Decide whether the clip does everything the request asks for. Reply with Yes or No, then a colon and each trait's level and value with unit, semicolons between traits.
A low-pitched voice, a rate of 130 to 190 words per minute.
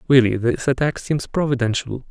Yes: low, 125 Hz; average, 140 wpm